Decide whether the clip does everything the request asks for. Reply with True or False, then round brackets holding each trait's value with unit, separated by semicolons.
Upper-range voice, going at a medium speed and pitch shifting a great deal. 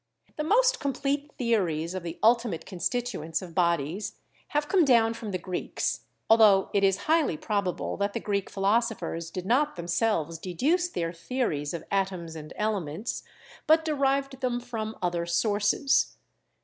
True (205 Hz; 150 wpm; 6.6 semitones)